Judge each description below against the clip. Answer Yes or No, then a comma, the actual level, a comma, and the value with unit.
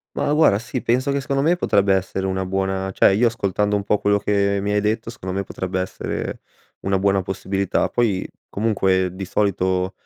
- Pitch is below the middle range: Yes, low, 100 Hz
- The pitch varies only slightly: Yes, narrow, 2.0 semitones